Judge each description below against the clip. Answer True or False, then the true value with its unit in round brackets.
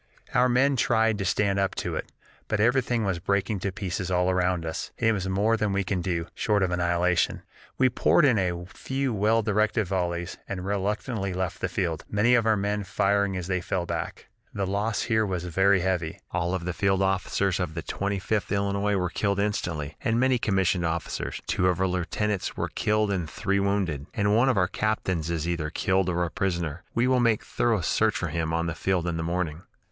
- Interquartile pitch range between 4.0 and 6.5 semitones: False (3.1 semitones)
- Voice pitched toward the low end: True (95 Hz)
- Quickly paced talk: True (210 wpm)